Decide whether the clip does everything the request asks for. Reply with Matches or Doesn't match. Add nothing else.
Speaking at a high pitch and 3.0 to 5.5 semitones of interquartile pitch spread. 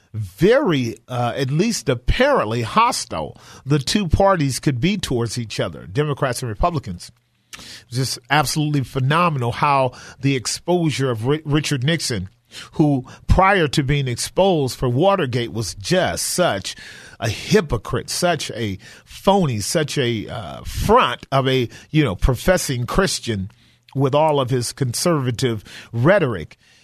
Doesn't match